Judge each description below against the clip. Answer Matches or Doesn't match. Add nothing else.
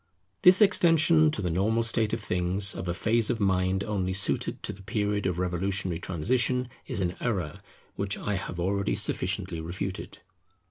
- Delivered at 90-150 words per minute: Doesn't match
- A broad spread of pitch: Doesn't match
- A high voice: Doesn't match